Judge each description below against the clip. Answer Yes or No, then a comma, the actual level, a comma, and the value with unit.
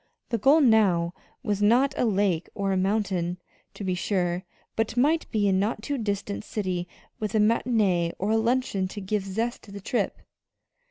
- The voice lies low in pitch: No, high, 205 Hz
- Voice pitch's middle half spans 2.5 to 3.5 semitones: Yes, average, 3.2 semitones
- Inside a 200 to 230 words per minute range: No, average, 180 wpm